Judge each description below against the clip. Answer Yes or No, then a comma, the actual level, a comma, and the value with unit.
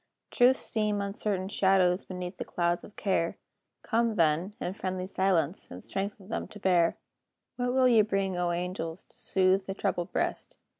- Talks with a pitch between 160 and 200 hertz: Yes, high, 190 Hz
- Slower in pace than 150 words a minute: No, average, 165 wpm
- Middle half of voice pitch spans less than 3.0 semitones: Yes, narrow, 2.5 semitones